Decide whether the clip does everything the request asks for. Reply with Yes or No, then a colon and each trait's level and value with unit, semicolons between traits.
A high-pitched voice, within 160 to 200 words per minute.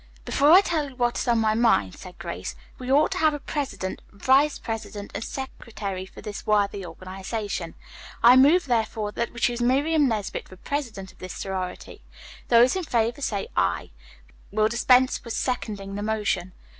Yes: high, 225 Hz; average, 175 wpm